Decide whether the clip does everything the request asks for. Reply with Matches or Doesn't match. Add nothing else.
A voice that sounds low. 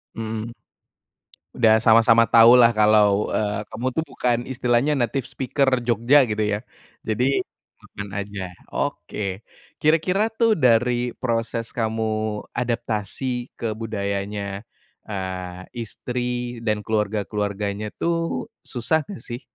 Matches